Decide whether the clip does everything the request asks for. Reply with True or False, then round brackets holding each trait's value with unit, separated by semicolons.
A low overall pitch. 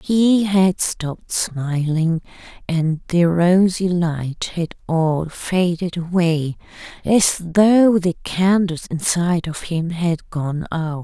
False (170 Hz)